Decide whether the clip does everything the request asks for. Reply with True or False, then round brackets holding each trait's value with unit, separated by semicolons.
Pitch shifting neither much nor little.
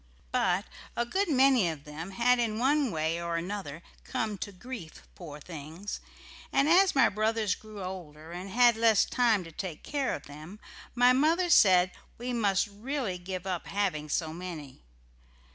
False (6.2 semitones)